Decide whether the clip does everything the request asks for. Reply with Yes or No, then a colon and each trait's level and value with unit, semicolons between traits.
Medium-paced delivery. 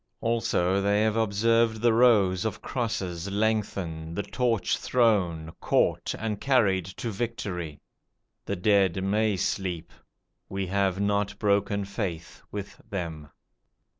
No: slow, 120 wpm